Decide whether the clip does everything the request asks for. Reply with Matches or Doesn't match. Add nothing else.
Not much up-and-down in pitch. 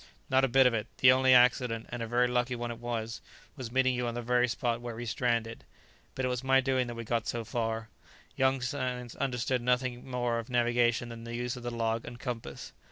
Matches